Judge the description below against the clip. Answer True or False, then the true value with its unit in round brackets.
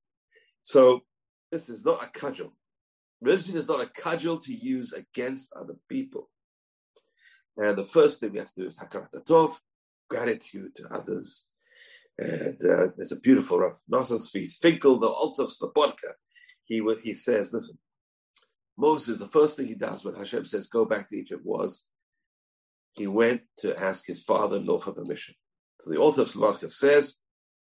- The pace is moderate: True (165 wpm)